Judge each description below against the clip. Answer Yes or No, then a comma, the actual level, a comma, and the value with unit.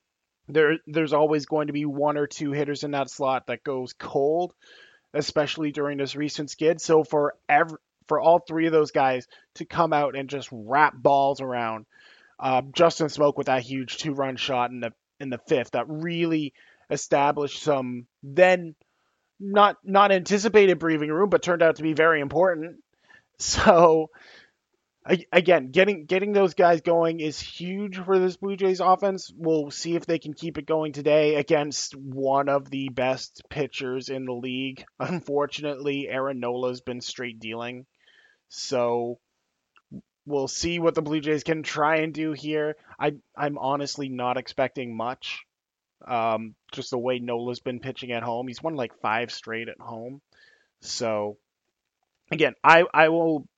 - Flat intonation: No, average, 3.8 semitones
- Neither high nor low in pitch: Yes, medium, 145 Hz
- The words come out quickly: No, average, 165 wpm